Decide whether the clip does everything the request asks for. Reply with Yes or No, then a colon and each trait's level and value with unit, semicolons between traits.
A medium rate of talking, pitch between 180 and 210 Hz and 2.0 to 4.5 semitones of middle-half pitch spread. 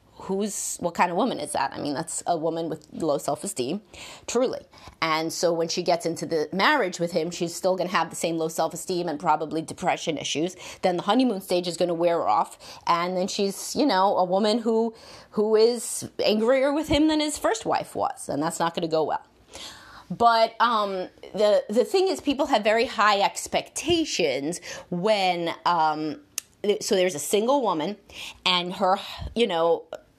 No: average, 190 wpm; medium, 185 Hz; average, 5.1 semitones